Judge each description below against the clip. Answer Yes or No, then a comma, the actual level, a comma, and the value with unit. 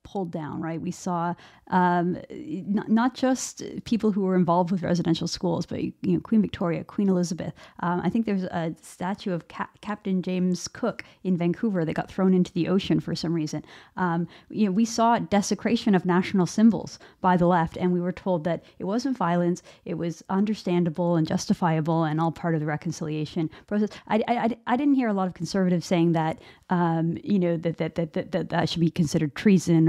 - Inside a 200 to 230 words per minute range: Yes, fast, 205 wpm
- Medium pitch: Yes, medium, 180 Hz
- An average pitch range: Yes, average, 3.0 semitones